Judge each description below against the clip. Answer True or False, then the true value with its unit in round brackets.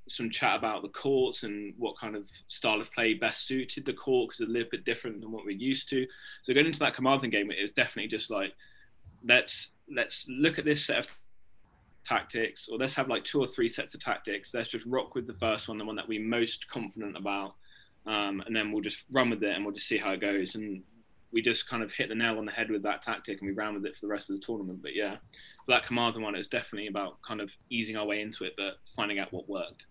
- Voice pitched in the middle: False (110 Hz)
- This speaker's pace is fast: True (260 wpm)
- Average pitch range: True (3.9 semitones)